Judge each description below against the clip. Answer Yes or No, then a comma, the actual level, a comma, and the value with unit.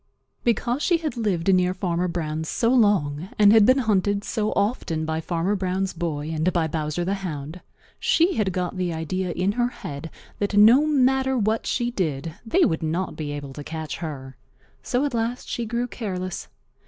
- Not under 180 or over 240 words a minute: Yes, average, 185 wpm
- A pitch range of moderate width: No, wide, 6.0 semitones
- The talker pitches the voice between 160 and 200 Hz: Yes, medium, 185 Hz